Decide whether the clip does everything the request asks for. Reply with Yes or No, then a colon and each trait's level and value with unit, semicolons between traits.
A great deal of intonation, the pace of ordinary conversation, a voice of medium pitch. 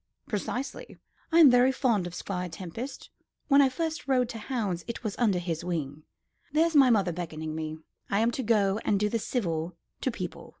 No: wide, 6.4 semitones; average, 190 wpm; high, 210 Hz